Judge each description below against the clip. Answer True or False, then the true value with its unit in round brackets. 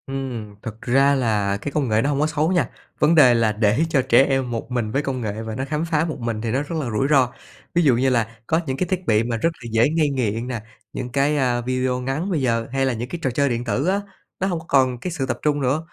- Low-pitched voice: True (130 Hz)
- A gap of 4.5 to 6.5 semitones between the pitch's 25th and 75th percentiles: False (4.1 semitones)